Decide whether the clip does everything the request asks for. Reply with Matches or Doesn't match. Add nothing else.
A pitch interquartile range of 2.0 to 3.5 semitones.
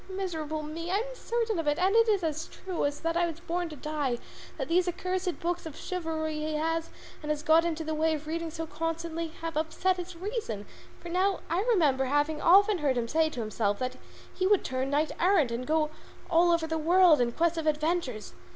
Matches